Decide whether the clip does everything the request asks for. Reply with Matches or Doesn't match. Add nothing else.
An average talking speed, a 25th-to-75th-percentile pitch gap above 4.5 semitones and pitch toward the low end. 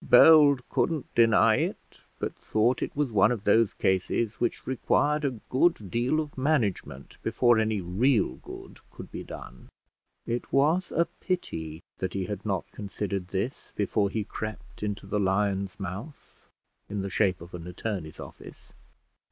Matches